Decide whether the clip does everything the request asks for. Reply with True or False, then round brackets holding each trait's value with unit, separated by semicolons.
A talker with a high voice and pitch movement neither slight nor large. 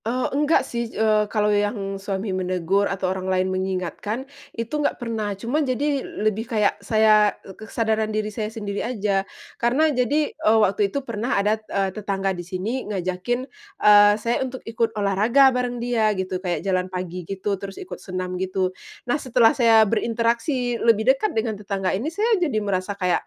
True (215 Hz; 3.7 semitones)